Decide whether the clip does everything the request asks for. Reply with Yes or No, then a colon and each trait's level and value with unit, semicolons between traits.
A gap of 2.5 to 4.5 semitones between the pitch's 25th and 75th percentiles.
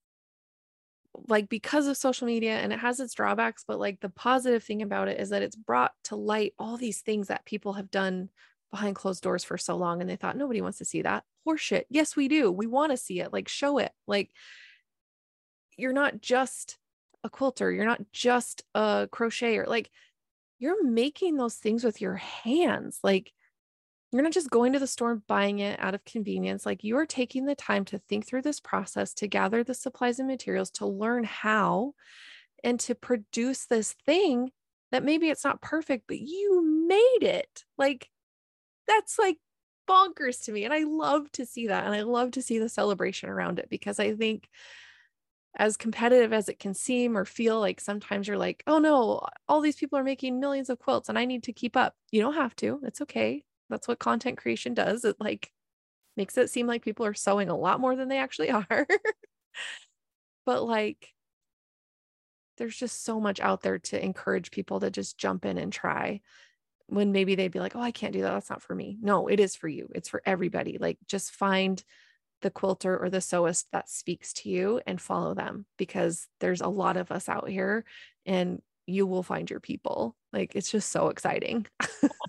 No: average, 5.0 semitones